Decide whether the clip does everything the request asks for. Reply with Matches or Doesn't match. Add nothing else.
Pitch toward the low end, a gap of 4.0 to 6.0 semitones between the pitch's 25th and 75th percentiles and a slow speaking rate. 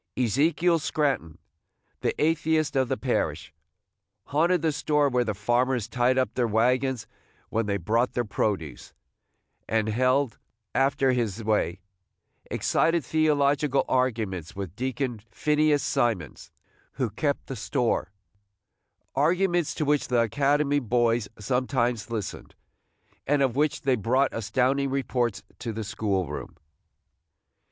Matches